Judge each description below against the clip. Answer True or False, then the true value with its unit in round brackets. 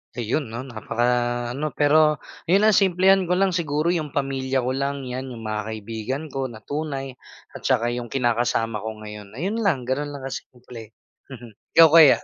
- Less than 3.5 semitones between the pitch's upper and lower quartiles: False (4.4 semitones)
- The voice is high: False (135 Hz)